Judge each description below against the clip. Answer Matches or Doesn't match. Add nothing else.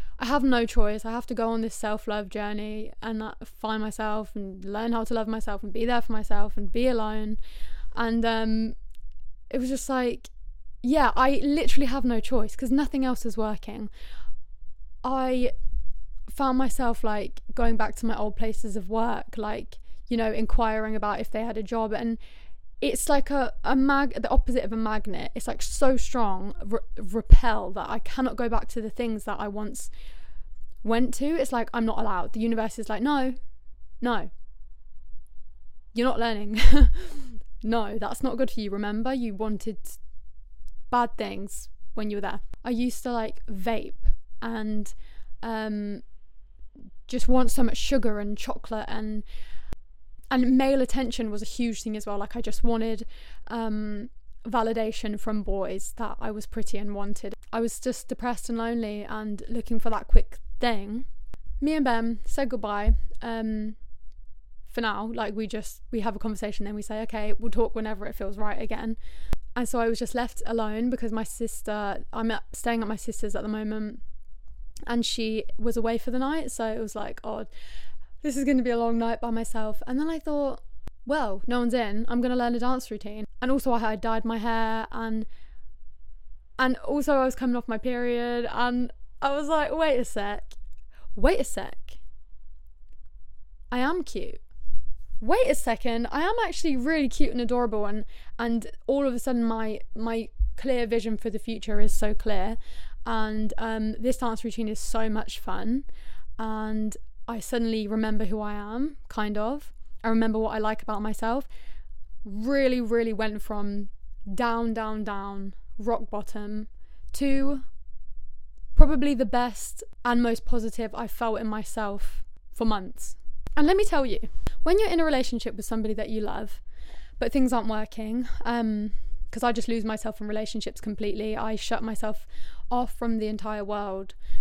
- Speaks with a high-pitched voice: Matches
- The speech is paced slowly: Doesn't match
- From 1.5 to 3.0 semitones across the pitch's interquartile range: Matches